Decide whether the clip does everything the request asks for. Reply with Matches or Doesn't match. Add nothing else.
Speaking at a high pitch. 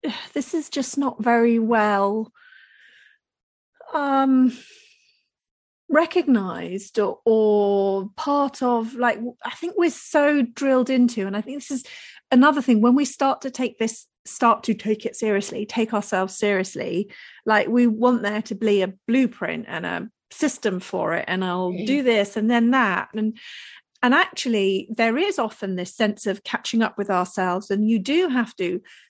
Matches